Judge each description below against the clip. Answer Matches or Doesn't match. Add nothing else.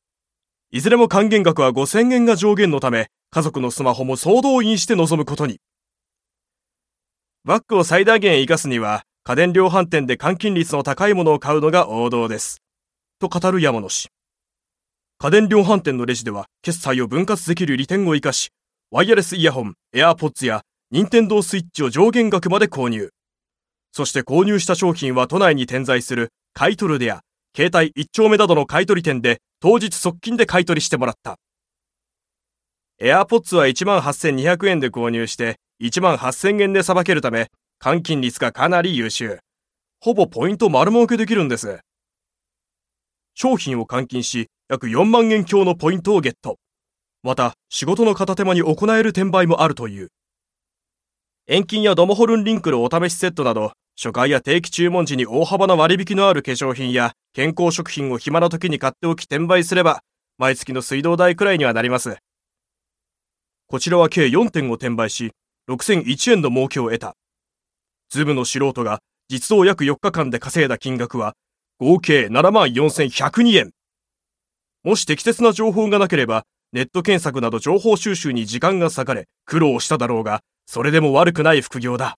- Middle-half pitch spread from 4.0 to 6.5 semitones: Doesn't match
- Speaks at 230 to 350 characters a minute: Matches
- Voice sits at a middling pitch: Matches